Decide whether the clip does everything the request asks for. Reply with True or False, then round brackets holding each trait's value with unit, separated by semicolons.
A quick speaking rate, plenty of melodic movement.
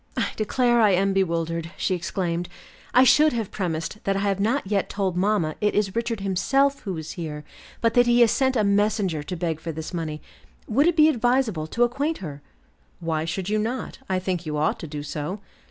True (210 wpm; 5.8 semitones)